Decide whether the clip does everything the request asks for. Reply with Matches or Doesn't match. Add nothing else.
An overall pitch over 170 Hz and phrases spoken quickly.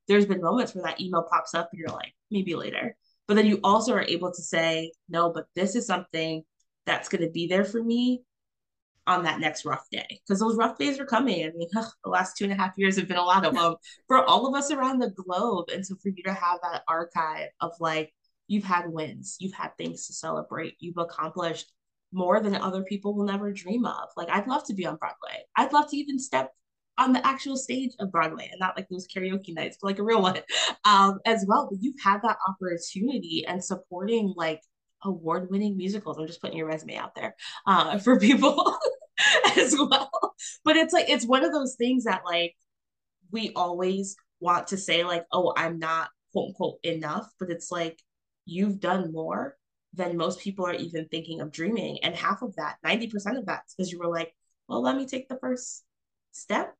Matches